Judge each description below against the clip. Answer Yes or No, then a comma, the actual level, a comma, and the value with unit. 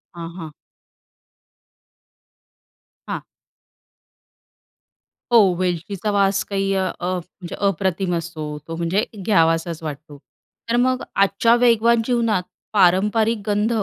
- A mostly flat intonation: No, average, 4.1 semitones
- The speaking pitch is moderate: No, high, 195 Hz